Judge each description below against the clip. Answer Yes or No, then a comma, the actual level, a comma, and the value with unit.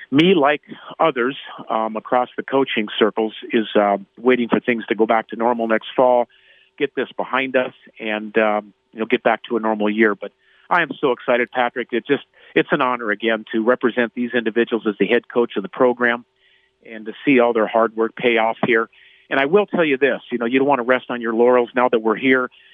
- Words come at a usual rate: No, fast, 230 wpm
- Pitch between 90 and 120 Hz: Yes, low, 115 Hz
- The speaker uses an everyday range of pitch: No, narrow, 2.0 semitones